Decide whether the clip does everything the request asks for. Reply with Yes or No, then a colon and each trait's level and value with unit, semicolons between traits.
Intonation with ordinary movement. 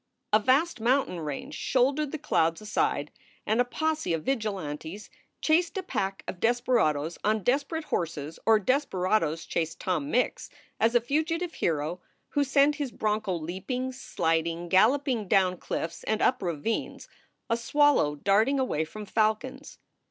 No: wide, 7.8 semitones